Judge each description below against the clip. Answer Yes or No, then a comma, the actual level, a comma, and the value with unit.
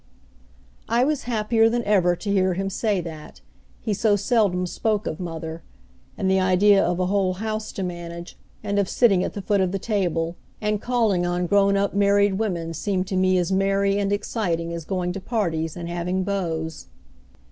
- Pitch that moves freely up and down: No, narrow, 2.6 semitones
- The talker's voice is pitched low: No, high, 190 Hz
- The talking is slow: No, average, 190 wpm